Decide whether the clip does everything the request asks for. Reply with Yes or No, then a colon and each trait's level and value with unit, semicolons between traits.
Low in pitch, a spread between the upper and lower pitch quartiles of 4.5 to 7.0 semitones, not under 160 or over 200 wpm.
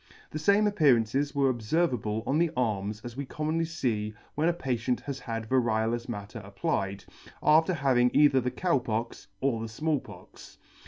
Yes: low, 125 Hz; average, 5.2 semitones; average, 170 wpm